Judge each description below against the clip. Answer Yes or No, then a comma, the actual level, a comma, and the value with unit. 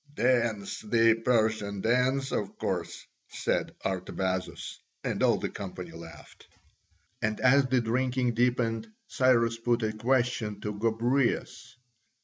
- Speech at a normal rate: No, slow, 120 wpm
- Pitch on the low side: Yes, low, 115 Hz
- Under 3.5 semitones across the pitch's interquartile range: Yes, average, 2.8 semitones